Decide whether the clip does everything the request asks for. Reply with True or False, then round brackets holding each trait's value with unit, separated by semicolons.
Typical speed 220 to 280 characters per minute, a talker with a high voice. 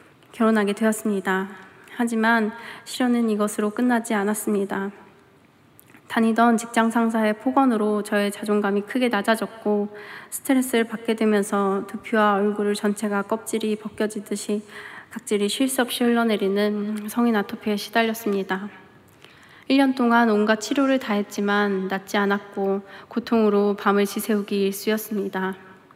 False (310 characters per minute; 210 Hz)